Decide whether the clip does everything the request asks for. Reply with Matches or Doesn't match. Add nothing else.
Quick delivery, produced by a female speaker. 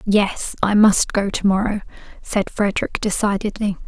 Doesn't match